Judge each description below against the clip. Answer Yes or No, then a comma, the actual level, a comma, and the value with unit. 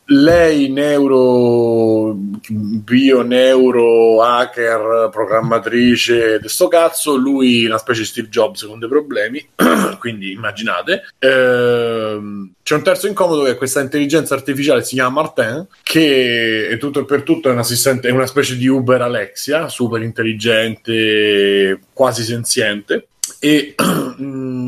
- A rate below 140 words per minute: Yes, average, 130 wpm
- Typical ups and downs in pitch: Yes, average, 3.5 semitones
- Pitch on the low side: Yes, low, 120 Hz